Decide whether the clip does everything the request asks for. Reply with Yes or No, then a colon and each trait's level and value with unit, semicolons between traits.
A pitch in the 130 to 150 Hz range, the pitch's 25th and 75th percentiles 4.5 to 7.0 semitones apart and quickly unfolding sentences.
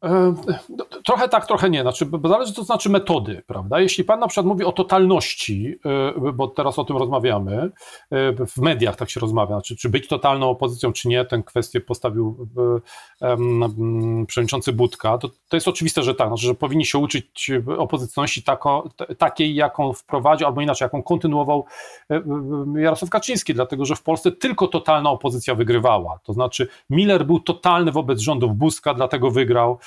Yes: medium, 140 Hz; average, 4.9 semitones; fast, 165 wpm